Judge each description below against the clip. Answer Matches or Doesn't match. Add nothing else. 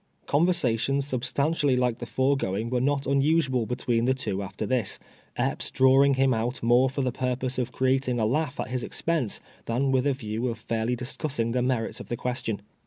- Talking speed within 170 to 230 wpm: Matches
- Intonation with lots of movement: Doesn't match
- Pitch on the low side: Matches